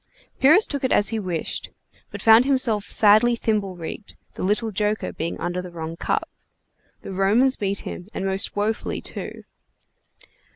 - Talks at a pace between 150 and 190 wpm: Yes, average, 165 wpm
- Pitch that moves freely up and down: No, average, 3.2 semitones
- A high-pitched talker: Yes, high, 210 Hz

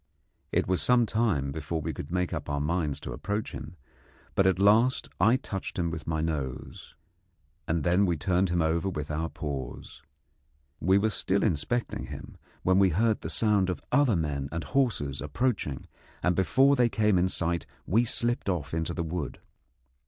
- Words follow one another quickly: No, average, 180 wpm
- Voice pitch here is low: Yes, very low, 90 Hz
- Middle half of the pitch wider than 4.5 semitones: Yes, average, 4.9 semitones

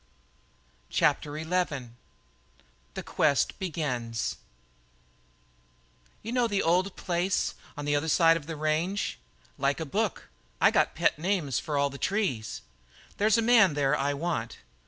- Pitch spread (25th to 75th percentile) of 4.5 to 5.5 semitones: Yes, average, 5.0 semitones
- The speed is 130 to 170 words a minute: Yes, slow, 135 wpm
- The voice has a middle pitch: Yes, medium, 160 Hz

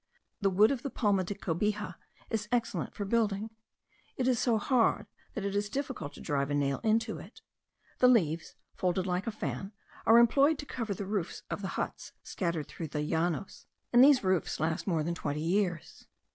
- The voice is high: Yes, high, 200 Hz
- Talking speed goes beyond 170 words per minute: Yes, average, 190 wpm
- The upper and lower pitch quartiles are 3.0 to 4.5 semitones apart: No, average, 5.0 semitones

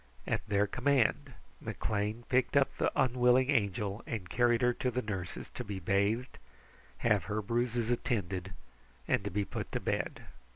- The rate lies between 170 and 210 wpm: No, average, 160 wpm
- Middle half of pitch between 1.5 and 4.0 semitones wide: Yes, average, 3.5 semitones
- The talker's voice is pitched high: No, low, 115 Hz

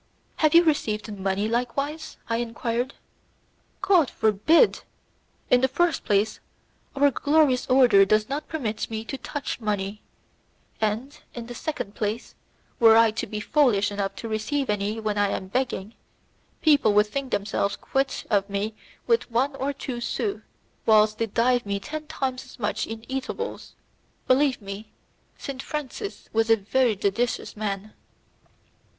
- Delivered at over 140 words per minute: Yes, average, 150 wpm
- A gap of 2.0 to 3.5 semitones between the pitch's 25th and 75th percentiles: No, average, 4.5 semitones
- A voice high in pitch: Yes, high, 230 Hz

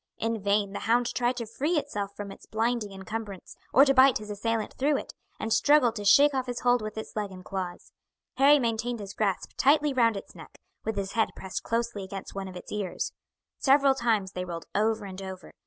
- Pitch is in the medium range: No, high, 220 Hz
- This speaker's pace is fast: Yes, fast, 215 wpm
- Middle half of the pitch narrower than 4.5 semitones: Yes, average, 3.8 semitones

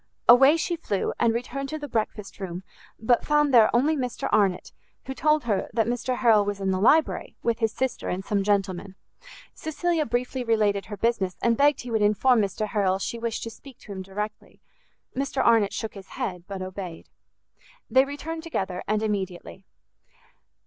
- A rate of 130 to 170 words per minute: No, average, 180 wpm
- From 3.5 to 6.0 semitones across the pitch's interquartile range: Yes, average, 4.7 semitones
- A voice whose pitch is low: No, high, 225 Hz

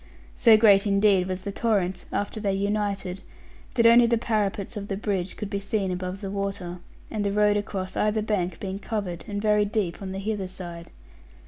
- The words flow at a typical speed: Yes, average, 190 wpm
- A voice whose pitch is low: No, high, 200 Hz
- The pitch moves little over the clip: Yes, narrow, 2.0 semitones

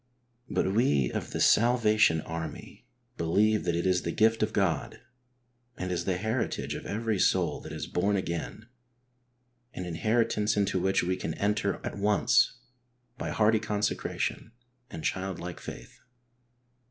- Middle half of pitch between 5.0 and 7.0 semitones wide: No, average, 3.5 semitones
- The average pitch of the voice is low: Yes, low, 100 Hz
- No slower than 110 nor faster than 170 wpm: Yes, average, 140 wpm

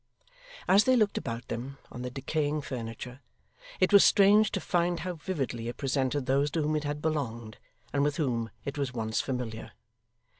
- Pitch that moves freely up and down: No, average, 4.4 semitones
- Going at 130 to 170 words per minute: No, average, 180 wpm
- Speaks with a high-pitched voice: No, medium, 140 Hz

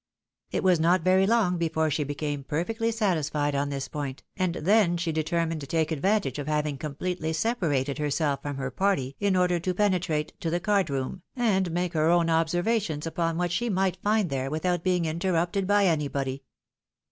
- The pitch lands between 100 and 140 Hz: No, medium, 165 Hz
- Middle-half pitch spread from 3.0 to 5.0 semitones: Yes, average, 3.8 semitones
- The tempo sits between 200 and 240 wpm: No, average, 180 wpm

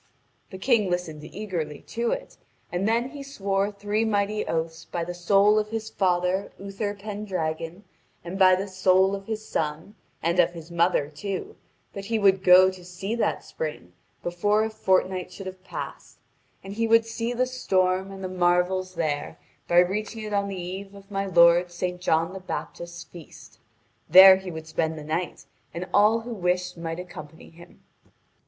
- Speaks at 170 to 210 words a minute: Yes, average, 175 wpm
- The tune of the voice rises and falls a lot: No, average, 2.9 semitones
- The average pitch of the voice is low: No, medium, 185 Hz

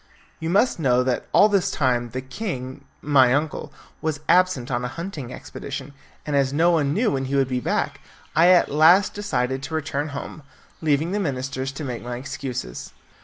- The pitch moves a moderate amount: Yes, average, 4.0 semitones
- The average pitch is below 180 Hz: Yes, medium, 140 Hz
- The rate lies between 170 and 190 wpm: Yes, average, 185 wpm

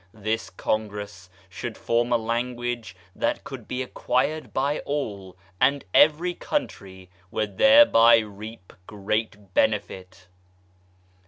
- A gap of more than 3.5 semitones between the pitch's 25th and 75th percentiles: Yes, average, 4.0 semitones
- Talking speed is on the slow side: Yes, slow, 105 wpm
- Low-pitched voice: Yes, low, 110 Hz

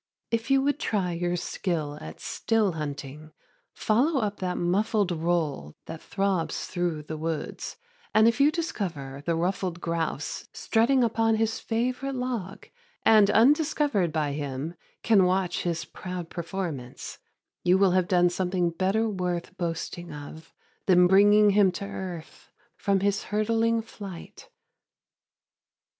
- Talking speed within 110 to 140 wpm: Yes, slow, 135 wpm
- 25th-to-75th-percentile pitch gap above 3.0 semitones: Yes, average, 4.6 semitones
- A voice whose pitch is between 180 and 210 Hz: Yes, medium, 185 Hz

